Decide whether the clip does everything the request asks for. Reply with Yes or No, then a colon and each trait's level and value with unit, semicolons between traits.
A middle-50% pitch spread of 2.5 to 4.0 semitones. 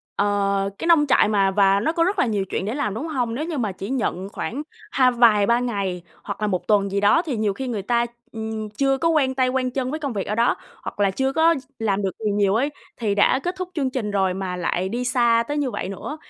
No: average, 5.0 semitones